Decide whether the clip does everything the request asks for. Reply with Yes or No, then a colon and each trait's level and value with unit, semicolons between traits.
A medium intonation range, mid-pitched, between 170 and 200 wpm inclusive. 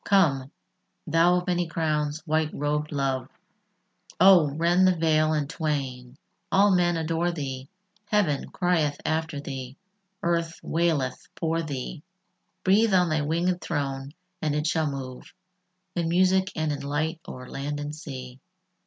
No: average, 3.2 semitones; medium, 155 Hz; average, 140 wpm